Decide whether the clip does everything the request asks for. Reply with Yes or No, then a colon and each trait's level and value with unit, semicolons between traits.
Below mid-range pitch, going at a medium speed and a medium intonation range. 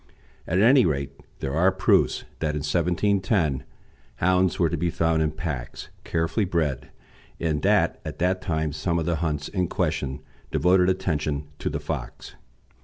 Yes: very low, 80 Hz; average, 160 wpm; average, 3.5 semitones